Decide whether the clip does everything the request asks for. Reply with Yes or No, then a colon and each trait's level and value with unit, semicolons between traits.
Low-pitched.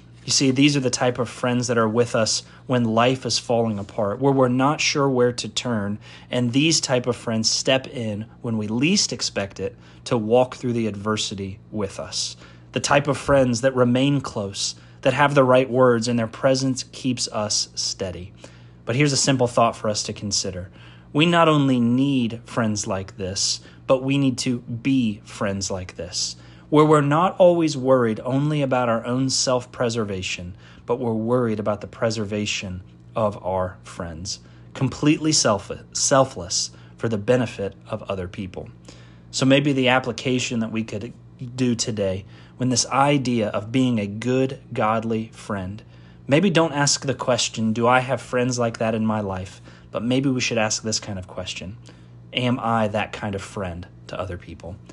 Yes: low, 115 Hz